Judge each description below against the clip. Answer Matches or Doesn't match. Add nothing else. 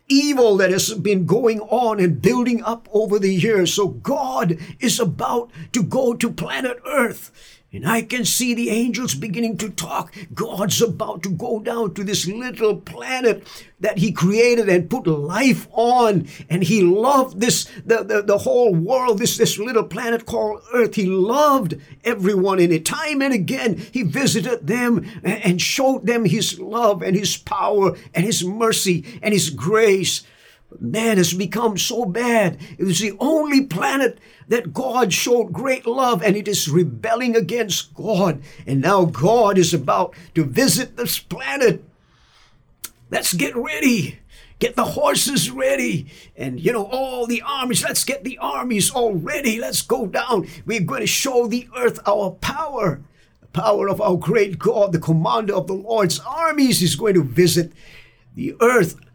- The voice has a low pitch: Doesn't match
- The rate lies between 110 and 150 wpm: Doesn't match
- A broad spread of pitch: Doesn't match